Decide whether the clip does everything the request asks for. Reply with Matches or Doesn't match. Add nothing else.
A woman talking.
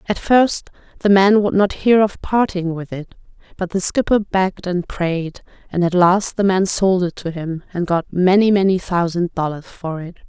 Matches